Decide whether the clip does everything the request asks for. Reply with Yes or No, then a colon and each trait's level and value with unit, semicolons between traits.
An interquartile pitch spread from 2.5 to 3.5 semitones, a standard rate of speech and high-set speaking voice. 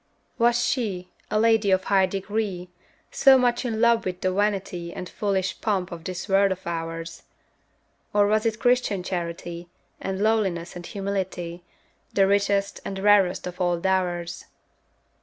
Yes: average, 2.9 semitones; average, 150 wpm; high, 195 Hz